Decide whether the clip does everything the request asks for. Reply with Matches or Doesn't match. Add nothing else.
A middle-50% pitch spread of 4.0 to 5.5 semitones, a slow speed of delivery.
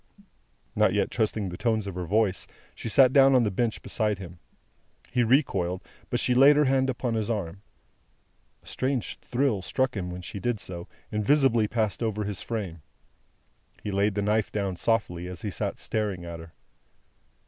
Doesn't match